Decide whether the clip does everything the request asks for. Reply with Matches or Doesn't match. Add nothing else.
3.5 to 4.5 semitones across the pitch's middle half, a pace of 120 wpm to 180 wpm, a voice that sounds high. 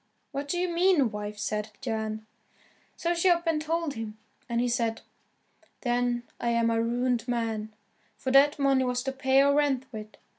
Matches